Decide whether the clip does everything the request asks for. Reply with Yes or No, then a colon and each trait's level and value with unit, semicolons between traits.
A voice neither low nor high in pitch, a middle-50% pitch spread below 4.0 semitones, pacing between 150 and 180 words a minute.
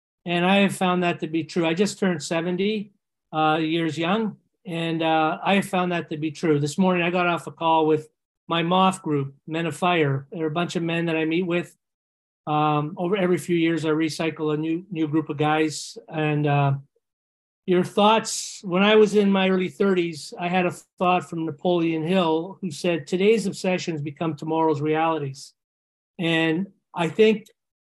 No: medium, 165 Hz; average, 2.8 semitones; average, 190 wpm